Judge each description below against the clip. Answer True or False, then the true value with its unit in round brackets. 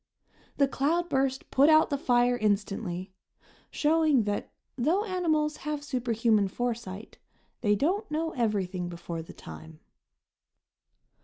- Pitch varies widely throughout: True (6.8 semitones)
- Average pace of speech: False (110 wpm)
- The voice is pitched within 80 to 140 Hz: False (245 Hz)